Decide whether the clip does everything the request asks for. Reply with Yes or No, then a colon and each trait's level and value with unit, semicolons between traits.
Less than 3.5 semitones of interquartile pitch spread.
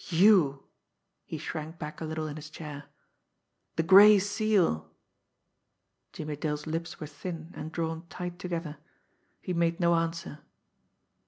Yes: narrow, 2.4 semitones